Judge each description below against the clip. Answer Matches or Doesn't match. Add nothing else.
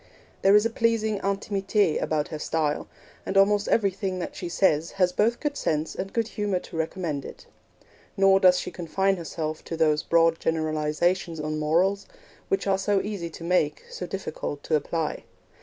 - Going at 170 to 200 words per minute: Matches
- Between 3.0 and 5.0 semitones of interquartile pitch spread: Matches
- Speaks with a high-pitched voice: Doesn't match